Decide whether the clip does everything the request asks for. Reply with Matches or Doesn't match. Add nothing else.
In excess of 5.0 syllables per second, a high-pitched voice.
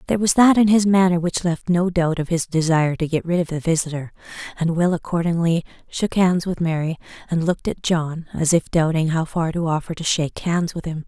Doesn't match